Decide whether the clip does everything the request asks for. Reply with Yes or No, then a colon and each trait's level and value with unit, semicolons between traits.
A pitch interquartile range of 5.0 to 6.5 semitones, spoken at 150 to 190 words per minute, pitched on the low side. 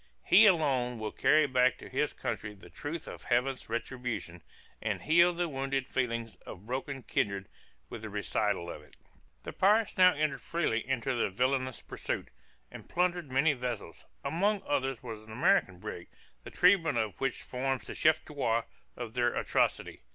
Yes: wide, 5.4 semitones; average, 165 wpm; low, 130 Hz